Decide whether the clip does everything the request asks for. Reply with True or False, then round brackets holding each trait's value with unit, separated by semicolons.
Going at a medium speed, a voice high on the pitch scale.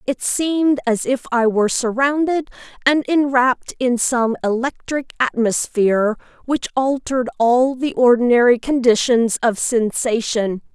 False (115 wpm; 250 Hz)